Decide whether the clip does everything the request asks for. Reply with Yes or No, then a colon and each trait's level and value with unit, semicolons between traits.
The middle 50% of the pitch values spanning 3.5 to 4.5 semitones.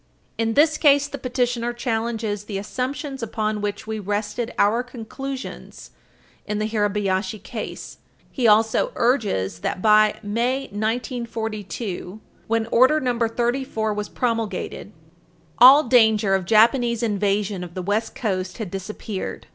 No: average, 2.9 semitones